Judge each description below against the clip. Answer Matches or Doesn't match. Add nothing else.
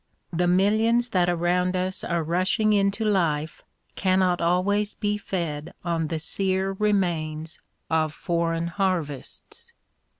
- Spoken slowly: Matches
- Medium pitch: Matches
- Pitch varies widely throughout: Doesn't match